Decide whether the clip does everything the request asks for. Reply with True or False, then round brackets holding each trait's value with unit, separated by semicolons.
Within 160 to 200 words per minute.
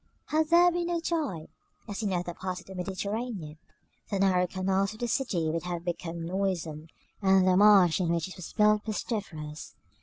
True (185 wpm)